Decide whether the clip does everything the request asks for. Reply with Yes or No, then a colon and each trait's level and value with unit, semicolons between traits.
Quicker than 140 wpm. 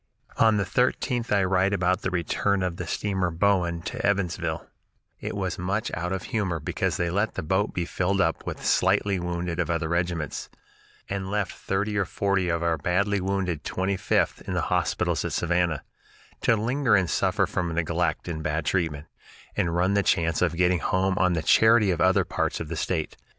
Yes: average, 190 wpm